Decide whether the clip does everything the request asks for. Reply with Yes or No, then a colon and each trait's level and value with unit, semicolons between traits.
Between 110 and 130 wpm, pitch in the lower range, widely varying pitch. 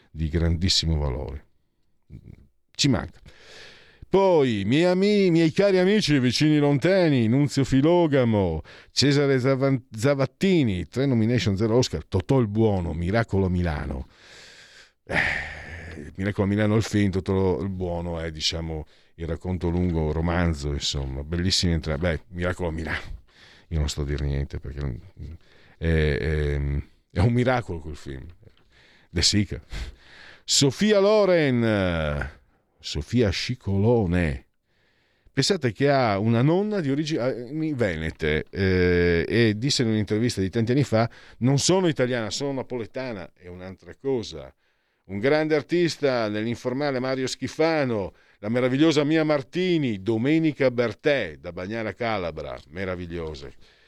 Yes: average, 125 wpm; low, 100 Hz; wide, 8.1 semitones